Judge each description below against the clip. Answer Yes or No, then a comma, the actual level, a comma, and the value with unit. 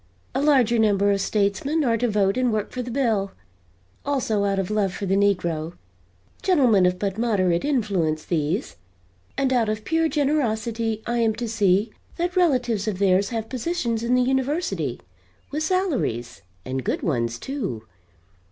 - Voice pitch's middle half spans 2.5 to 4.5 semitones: No, average, 4.9 semitones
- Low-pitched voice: No, high, 220 Hz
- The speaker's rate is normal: Yes, average, 160 wpm